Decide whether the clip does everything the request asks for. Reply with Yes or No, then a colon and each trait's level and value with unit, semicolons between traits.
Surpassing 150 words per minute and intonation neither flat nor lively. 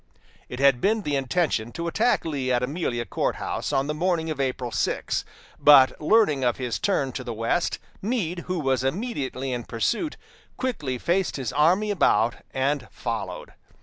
No: average, 170 wpm; wide, 5.9 semitones